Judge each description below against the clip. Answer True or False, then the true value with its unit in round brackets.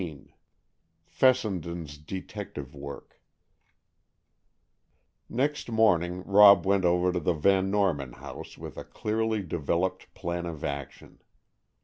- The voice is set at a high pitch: False (90 Hz)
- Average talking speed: False (105 wpm)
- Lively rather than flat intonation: False (4.3 semitones)